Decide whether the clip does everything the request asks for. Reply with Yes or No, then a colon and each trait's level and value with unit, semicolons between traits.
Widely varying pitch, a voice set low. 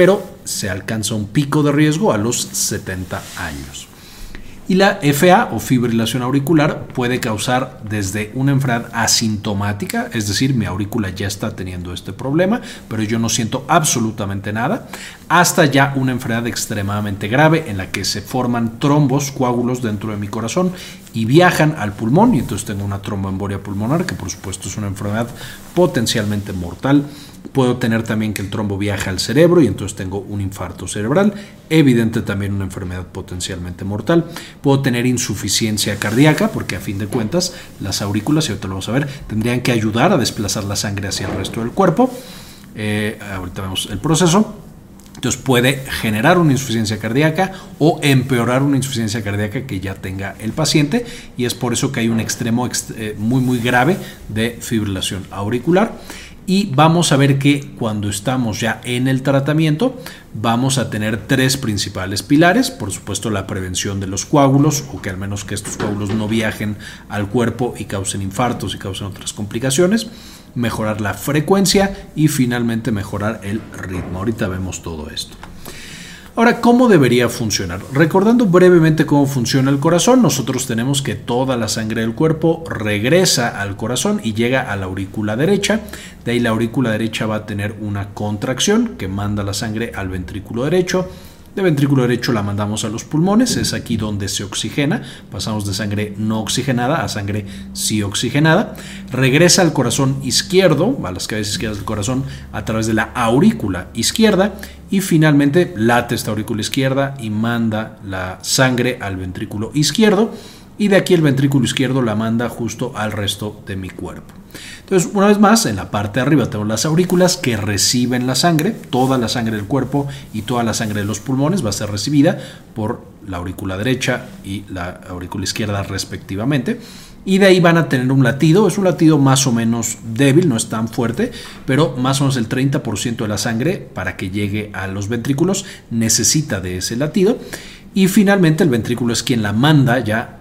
Yes: wide, 5.8 semitones; low, 115 Hz